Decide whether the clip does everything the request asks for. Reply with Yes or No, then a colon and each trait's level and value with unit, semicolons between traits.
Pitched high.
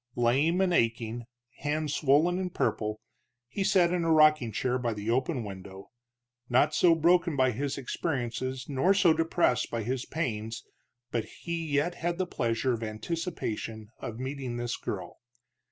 No: low, 135 Hz